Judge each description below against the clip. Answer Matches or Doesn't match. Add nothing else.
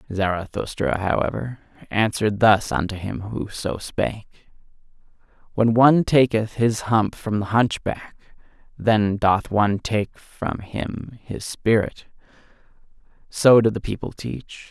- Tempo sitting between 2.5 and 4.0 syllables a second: Matches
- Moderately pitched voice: Doesn't match